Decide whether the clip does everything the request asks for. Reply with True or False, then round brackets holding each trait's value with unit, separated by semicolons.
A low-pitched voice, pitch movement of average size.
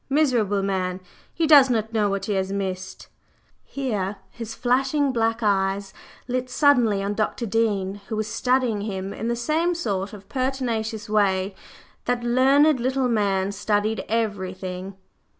False (220 Hz; 4.2 semitones)